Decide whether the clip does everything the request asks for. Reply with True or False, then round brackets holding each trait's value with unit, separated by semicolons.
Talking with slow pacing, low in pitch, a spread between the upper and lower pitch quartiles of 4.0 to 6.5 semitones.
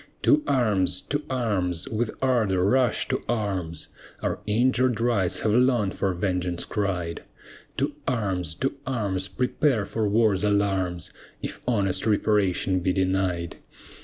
True (130 wpm; 100 Hz; 4.4 semitones)